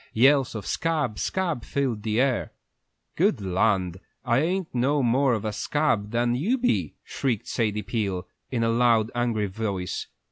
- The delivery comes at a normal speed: Yes, average, 155 wpm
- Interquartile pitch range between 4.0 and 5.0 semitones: Yes, average, 4.7 semitones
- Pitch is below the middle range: Yes, low, 115 Hz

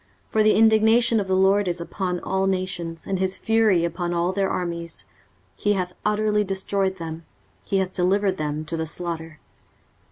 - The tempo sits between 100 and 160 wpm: No, average, 180 wpm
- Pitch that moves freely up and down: No, average, 3.0 semitones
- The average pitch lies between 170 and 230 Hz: Yes, medium, 185 Hz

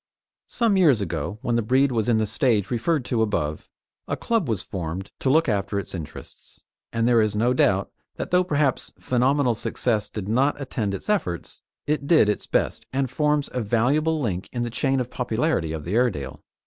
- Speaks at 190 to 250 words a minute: Yes, average, 195 wpm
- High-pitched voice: No, low, 120 Hz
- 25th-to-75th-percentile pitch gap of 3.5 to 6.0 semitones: Yes, average, 5.3 semitones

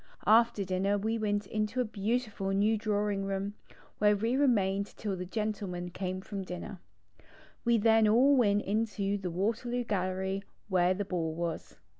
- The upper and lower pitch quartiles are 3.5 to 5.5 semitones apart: No, narrow, 2.5 semitones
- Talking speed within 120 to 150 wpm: No, average, 160 wpm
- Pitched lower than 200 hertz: No, high, 205 Hz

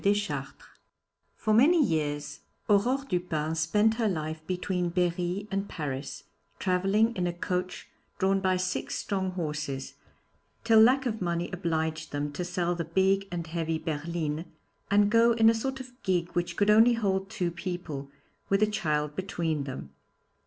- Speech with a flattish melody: No, average, 4.2 semitones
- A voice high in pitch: No, medium, 180 Hz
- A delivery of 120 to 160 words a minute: Yes, average, 155 wpm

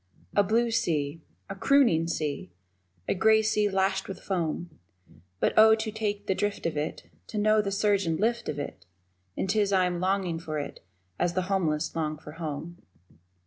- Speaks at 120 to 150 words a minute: No, average, 185 wpm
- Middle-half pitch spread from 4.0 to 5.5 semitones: Yes, average, 4.4 semitones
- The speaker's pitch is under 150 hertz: No, high, 190 Hz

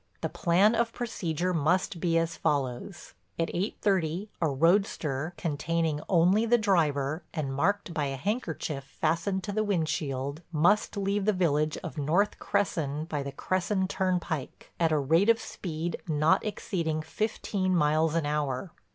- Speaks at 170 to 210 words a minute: No, average, 150 wpm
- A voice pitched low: No, medium, 165 Hz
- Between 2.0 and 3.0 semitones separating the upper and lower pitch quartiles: No, average, 4.2 semitones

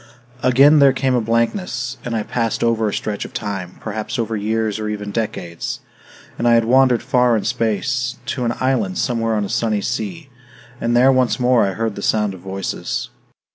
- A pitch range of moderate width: Yes, average, 3.0 semitones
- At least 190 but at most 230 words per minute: Yes, average, 200 wpm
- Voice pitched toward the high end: No, low, 115 Hz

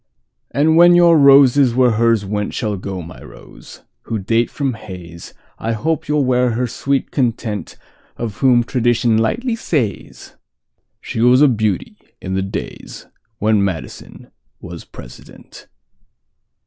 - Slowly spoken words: Yes, slow, 120 wpm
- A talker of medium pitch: No, low, 115 Hz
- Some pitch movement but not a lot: Yes, average, 4.6 semitones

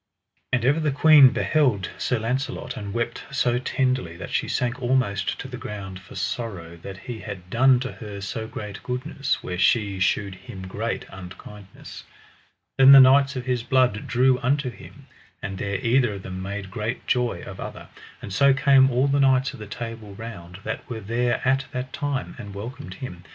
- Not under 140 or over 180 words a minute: No, average, 190 wpm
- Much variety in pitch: No, average, 4.7 semitones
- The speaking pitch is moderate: No, low, 120 Hz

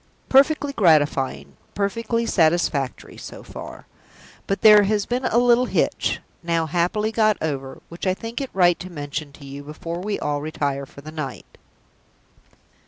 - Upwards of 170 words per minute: No, average, 155 wpm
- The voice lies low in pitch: No, medium, 170 Hz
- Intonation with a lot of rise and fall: Yes, wide, 6.8 semitones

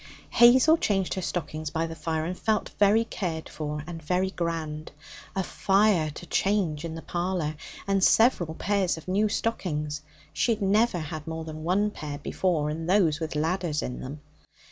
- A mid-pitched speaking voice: Yes, medium, 170 Hz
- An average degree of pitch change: Yes, average, 4.0 semitones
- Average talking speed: Yes, average, 175 wpm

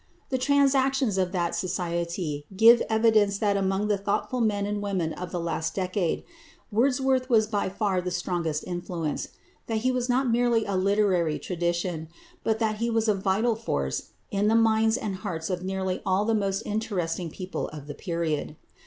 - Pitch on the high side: Yes, high, 200 Hz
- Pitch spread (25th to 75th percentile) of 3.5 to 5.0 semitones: Yes, average, 4.1 semitones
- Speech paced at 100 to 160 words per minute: No, average, 175 wpm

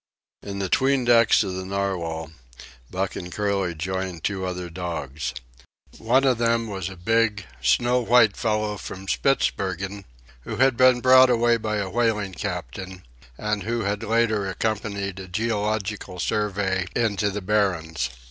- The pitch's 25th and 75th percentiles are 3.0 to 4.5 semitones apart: Yes, average, 3.4 semitones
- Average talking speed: Yes, average, 150 wpm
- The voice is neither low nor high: No, low, 100 Hz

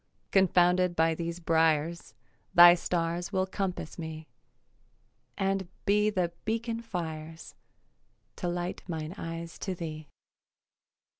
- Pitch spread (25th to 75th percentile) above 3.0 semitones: No, narrow, 2.5 semitones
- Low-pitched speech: No, medium, 175 Hz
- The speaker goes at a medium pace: No, slow, 105 wpm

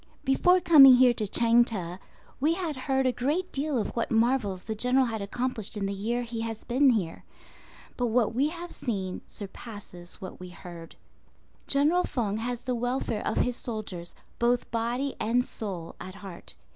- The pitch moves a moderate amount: Yes, average, 4.1 semitones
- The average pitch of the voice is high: Yes, high, 235 Hz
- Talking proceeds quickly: No, average, 175 wpm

